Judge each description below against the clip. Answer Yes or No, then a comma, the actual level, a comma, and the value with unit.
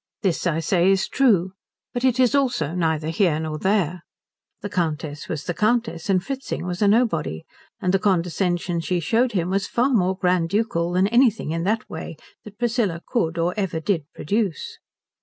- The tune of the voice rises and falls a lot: No, average, 4.5 semitones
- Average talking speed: Yes, average, 180 wpm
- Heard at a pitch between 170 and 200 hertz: Yes, medium, 185 Hz